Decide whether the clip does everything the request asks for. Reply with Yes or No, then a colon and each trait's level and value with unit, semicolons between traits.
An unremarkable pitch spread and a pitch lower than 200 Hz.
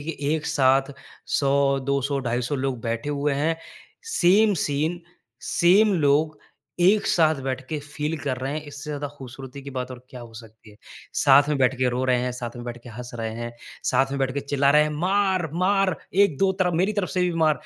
Yes: average, 3.8 semitones; medium, 140 Hz